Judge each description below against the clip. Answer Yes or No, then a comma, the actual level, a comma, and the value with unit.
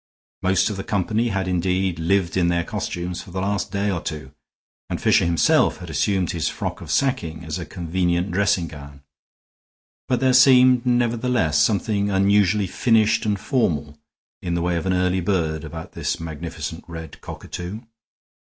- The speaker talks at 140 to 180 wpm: Yes, average, 165 wpm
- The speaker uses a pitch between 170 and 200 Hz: No, very low, 90 Hz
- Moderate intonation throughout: Yes, average, 3.6 semitones